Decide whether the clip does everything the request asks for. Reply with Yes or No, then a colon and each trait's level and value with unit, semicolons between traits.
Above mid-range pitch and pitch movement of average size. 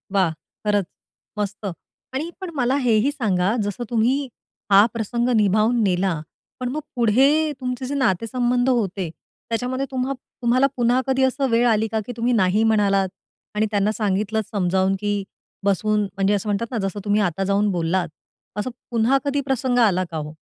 Yes: high, 220 Hz; average, 4.0 semitones